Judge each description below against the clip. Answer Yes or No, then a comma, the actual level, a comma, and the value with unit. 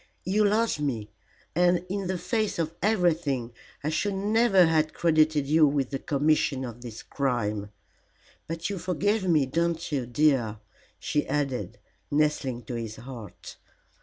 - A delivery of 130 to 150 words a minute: Yes, average, 145 wpm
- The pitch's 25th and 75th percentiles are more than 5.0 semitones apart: Yes, wide, 5.5 semitones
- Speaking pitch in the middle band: Yes, medium, 155 Hz